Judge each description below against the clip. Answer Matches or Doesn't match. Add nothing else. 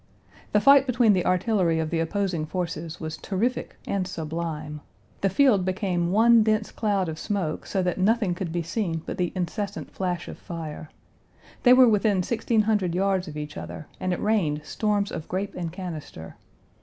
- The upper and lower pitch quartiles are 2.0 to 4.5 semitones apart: Matches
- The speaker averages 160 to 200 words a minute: Matches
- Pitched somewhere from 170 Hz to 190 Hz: Matches